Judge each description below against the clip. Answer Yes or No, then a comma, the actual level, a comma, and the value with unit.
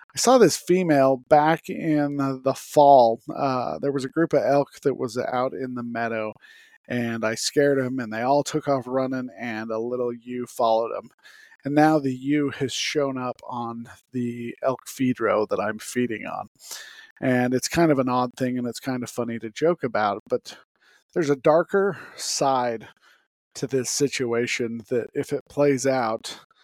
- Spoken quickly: No, average, 185 wpm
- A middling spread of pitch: Yes, average, 3.1 semitones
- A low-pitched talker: Yes, low, 130 Hz